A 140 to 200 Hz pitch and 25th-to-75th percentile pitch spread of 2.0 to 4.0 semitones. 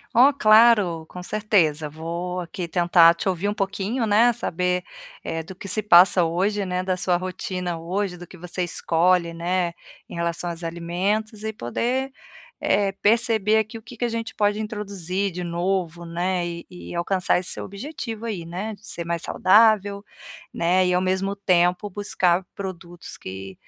Yes: medium, 185 Hz; average, 3.3 semitones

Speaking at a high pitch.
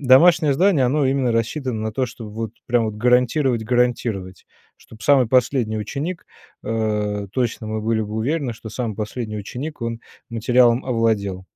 No: low, 115 Hz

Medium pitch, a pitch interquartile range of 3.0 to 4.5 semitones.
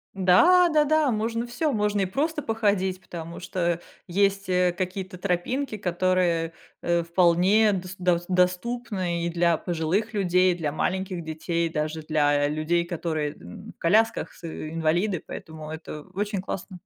Yes: medium, 180 Hz; average, 3.4 semitones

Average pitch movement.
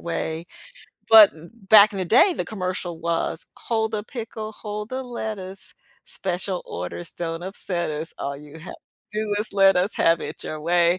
Yes: average, 4.1 semitones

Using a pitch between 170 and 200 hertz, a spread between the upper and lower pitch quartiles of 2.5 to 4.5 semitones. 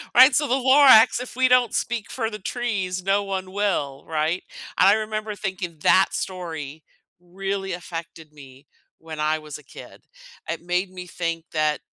No: medium, 185 Hz; average, 4.9 semitones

